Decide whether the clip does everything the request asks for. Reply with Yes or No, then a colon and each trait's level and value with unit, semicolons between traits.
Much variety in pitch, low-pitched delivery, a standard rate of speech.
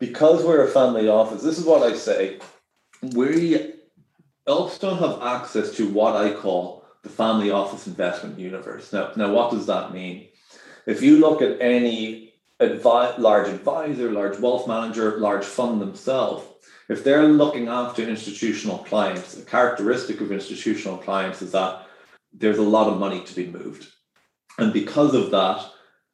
Yes: wide, 6.4 semitones; low, 115 Hz; average, 160 wpm